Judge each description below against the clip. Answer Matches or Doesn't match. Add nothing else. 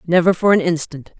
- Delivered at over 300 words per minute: Doesn't match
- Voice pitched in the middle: Matches